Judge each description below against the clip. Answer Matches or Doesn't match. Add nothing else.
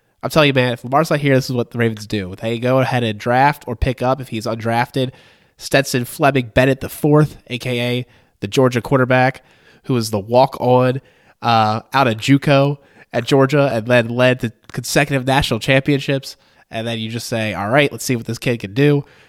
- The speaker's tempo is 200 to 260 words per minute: Matches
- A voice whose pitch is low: Matches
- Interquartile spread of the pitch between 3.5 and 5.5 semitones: Doesn't match